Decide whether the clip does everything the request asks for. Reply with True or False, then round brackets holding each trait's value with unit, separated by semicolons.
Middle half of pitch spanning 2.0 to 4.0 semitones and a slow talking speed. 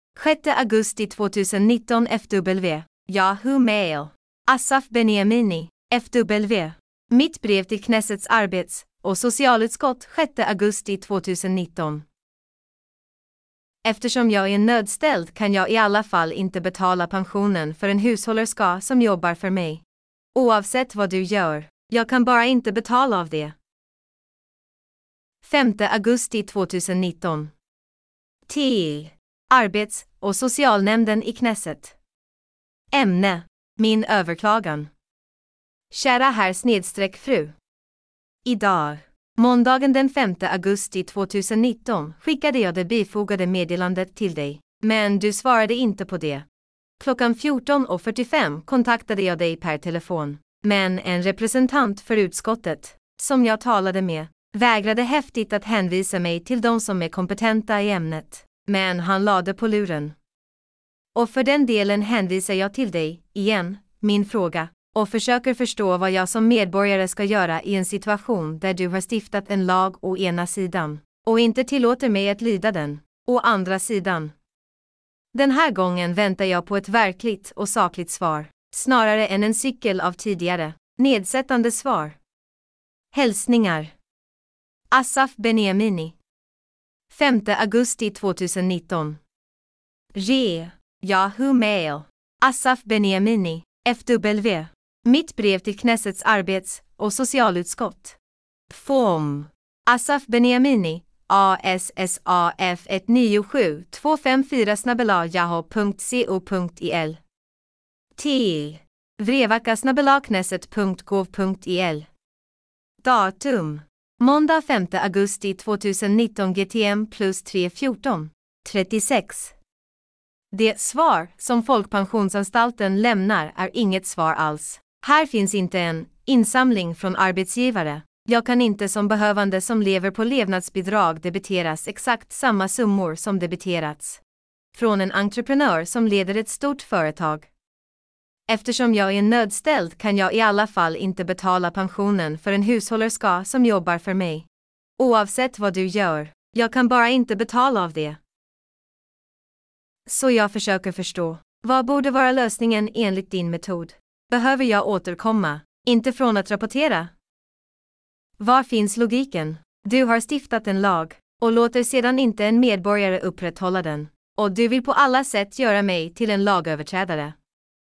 False (4.4 semitones; 115 wpm)